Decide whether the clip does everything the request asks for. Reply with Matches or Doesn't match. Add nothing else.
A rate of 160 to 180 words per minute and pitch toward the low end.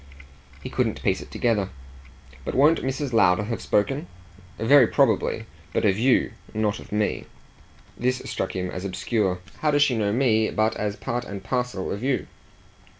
Matches